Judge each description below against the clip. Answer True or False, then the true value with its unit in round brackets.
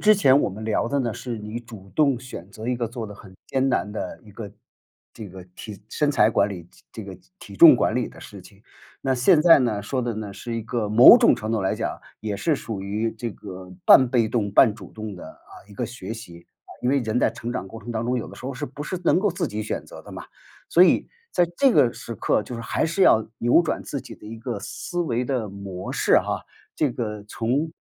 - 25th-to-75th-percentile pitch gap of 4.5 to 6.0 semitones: False (3.4 semitones)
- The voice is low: True (115 Hz)